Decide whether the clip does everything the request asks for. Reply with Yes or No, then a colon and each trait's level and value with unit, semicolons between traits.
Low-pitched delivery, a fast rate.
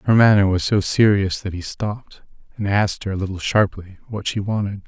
Yes: low, 100 Hz; fast, 210 wpm